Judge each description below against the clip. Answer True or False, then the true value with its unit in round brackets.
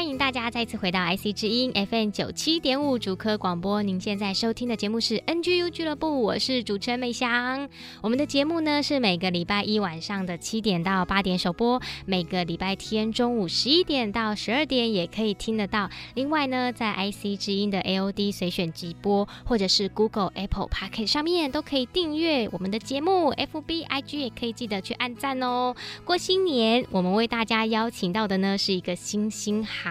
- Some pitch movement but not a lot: True (4.6 semitones)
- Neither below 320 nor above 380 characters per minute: True (335 characters per minute)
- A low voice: False (220 Hz)